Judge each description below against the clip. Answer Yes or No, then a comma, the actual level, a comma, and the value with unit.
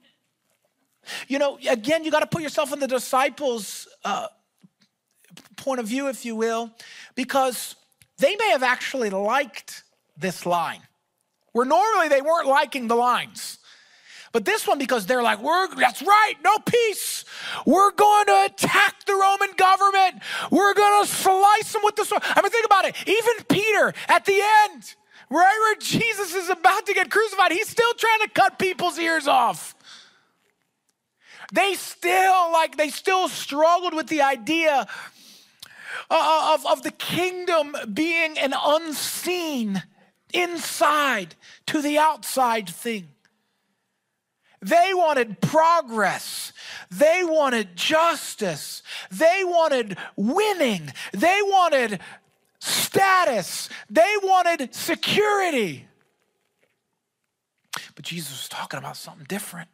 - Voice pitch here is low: No, very high, 320 Hz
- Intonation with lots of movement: Yes, wide, 7.3 semitones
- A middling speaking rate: No, slow, 130 wpm